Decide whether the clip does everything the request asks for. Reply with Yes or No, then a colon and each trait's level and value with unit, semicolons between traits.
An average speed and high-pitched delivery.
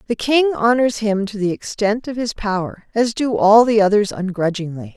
Yes: average, 195 wpm; high, 210 Hz